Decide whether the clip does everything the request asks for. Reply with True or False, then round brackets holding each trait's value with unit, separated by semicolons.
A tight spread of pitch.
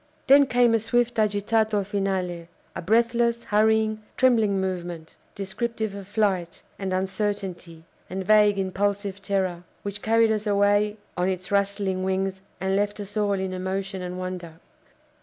True (2.3 semitones)